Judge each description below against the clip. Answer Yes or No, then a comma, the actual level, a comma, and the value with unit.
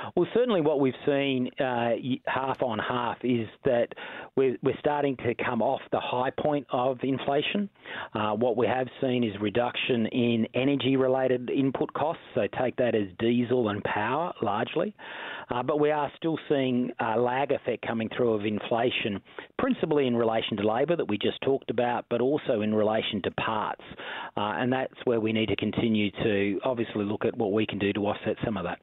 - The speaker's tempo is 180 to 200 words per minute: Yes, average, 190 wpm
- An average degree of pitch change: Yes, average, 3.4 semitones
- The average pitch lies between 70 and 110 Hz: No, low, 125 Hz